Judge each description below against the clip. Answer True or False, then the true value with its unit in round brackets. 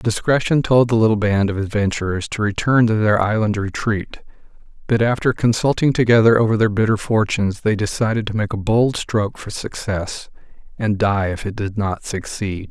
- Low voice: True (105 Hz)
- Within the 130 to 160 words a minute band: False (175 wpm)